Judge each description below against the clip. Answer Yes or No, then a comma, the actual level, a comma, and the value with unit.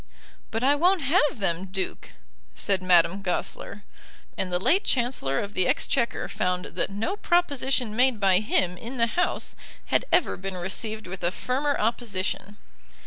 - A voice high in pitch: Yes, high, 210 Hz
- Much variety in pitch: Yes, wide, 6.0 semitones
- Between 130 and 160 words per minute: Yes, average, 155 wpm